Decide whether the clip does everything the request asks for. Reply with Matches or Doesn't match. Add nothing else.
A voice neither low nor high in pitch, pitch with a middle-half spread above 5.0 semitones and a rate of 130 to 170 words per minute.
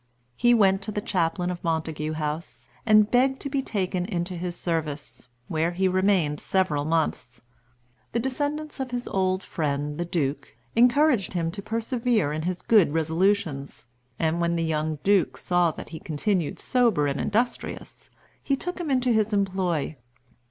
Matches